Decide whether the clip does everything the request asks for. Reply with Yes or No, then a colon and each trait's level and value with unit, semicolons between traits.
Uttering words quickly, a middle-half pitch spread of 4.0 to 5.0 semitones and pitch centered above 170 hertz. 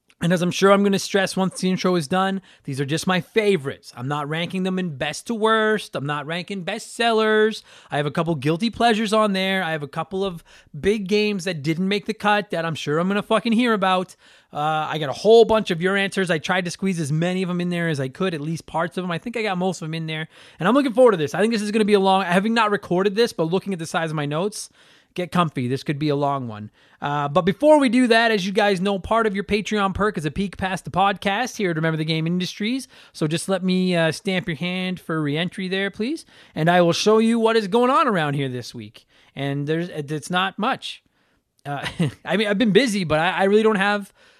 Yes: fast, 270 wpm; average, 4.4 semitones; medium, 185 Hz